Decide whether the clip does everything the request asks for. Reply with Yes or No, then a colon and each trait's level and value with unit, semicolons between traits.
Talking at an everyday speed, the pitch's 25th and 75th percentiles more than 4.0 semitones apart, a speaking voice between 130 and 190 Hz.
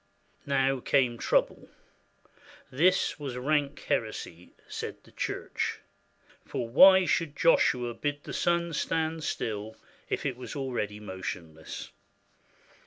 No: slow, 110 wpm; average, 5.1 semitones; low, 135 Hz